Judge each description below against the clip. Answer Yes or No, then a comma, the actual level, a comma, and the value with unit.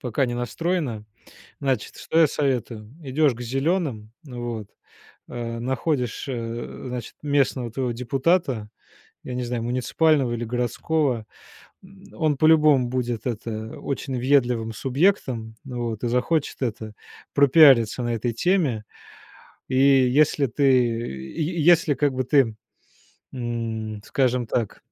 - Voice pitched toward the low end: Yes, low, 125 Hz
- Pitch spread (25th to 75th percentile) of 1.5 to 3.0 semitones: No, average, 3.4 semitones